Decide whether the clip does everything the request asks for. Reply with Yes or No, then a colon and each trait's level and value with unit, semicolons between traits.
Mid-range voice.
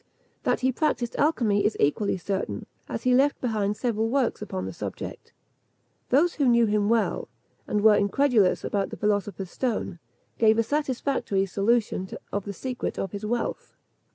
No: high, 220 Hz